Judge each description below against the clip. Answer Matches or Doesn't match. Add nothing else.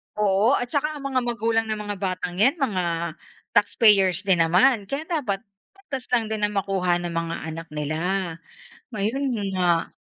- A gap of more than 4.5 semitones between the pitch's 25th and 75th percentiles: Matches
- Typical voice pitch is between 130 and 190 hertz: Doesn't match